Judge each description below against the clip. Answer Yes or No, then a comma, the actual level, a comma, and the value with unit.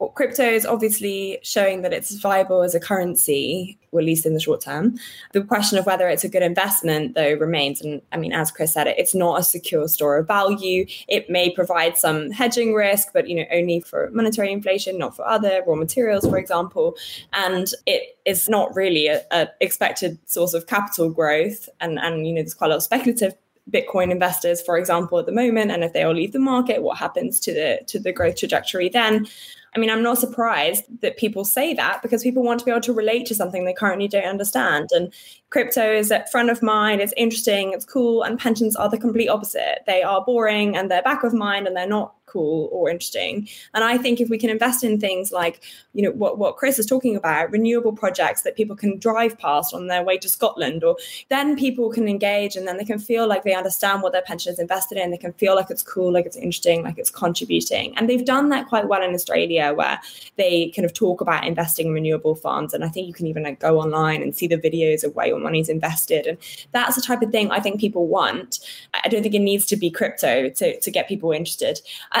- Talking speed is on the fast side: Yes, fast, 235 wpm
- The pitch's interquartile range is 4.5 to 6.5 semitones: Yes, average, 5.0 semitones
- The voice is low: No, high, 200 Hz